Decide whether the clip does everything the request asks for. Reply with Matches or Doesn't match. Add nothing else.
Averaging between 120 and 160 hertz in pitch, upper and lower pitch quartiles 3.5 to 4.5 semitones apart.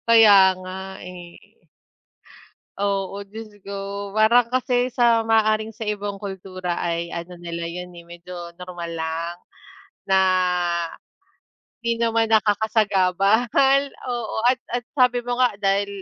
Doesn't match